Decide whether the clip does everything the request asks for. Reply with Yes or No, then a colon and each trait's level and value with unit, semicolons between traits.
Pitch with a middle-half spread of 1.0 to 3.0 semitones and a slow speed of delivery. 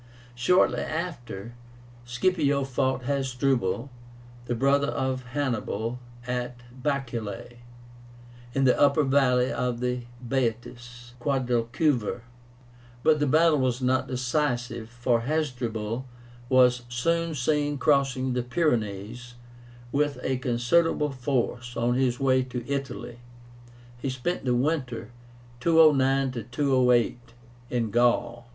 Yes: narrow, 2.5 semitones; slow, 105 wpm